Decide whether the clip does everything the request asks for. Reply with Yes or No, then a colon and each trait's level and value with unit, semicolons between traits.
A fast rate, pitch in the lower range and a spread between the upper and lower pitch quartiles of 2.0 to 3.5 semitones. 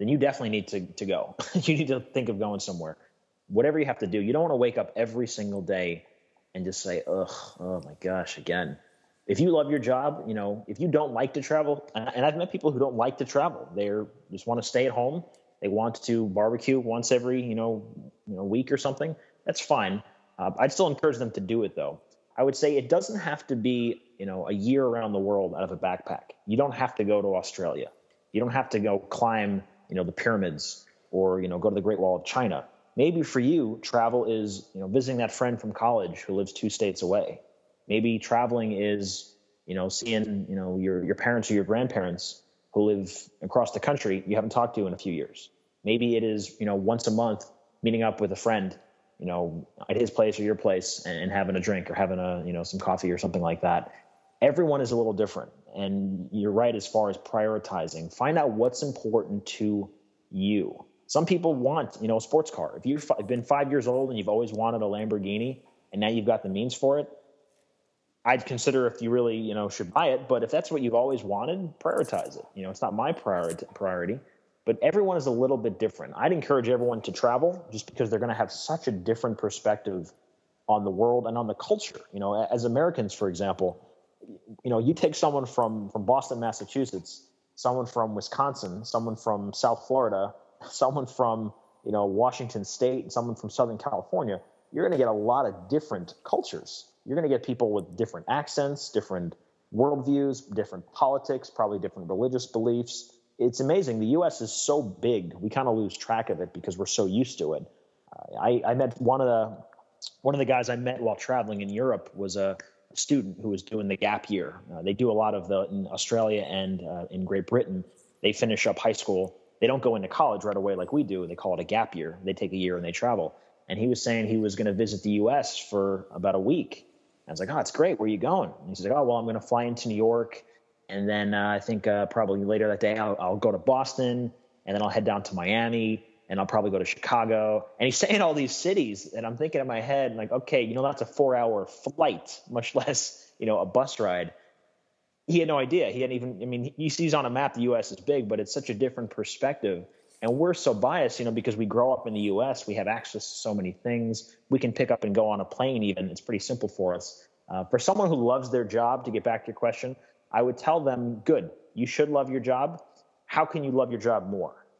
No: fast, 235 wpm; low, 115 Hz; average, 4.0 semitones